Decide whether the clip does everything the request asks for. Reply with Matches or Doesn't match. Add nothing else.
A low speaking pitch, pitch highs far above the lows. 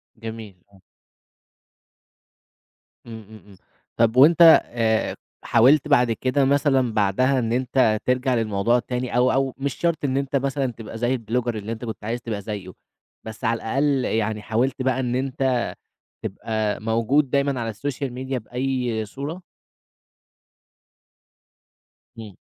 Doesn't match